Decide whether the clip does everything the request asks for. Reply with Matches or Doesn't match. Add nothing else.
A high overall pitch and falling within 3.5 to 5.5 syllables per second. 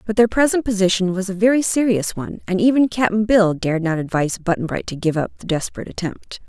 Doesn't match